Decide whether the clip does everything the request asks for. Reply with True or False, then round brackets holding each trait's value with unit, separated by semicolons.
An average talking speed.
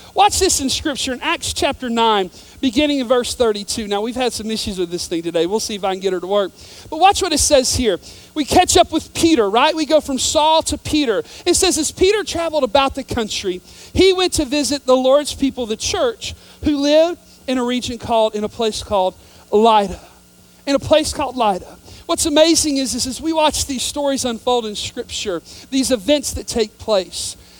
False (215 wpm)